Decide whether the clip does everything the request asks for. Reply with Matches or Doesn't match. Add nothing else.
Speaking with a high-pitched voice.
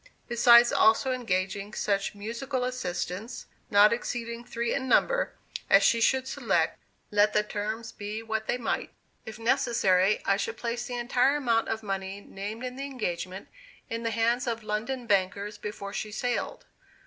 Matches